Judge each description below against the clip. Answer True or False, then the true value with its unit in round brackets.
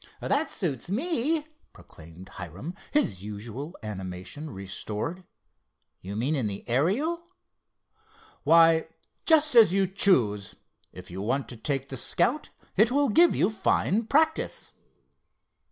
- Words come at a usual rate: False (120 wpm)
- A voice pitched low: False (150 Hz)